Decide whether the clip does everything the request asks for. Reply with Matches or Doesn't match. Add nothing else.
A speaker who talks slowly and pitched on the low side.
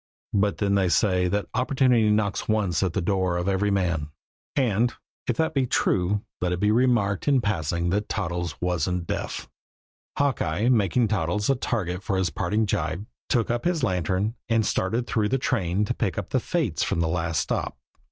Doesn't match